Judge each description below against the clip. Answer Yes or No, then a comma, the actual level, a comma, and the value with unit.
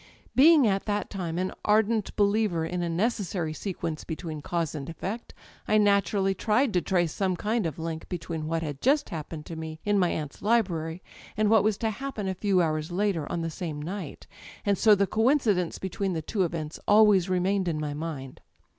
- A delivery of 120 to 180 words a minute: No, average, 190 wpm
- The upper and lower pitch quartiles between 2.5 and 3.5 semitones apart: No, average, 4.2 semitones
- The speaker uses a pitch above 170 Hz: Yes, medium, 185 Hz